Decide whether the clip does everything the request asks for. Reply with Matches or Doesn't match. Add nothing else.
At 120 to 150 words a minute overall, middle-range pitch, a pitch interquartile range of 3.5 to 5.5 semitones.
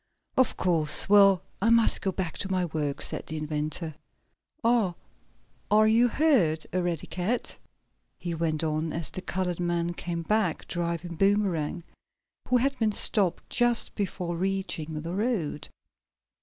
Matches